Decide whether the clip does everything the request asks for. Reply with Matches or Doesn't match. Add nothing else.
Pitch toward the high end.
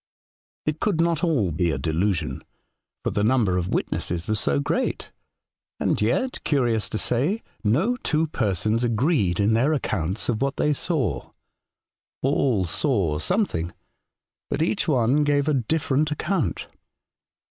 Doesn't match